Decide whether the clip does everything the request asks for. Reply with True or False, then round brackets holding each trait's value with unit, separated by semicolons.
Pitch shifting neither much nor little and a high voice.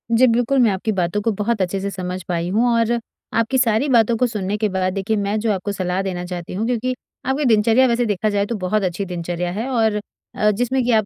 True (3.8 semitones; 210 Hz)